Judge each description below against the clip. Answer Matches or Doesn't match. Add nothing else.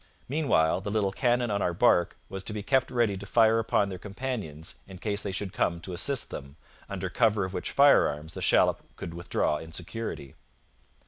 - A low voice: Matches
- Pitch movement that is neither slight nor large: Matches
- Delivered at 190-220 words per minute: Matches